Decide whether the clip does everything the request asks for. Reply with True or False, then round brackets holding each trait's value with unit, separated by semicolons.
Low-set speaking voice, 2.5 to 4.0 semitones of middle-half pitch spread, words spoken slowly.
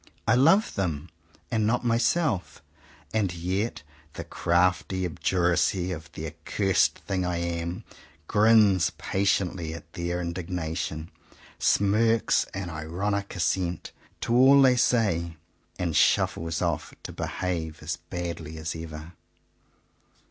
True (90 Hz; 3.6 semitones; 115 wpm)